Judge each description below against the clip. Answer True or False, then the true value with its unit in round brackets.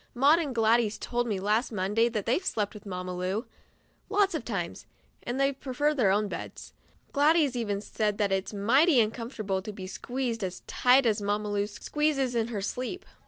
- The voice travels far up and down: False (4.3 semitones)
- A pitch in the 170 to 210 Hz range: False (225 Hz)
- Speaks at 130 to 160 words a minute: False (190 wpm)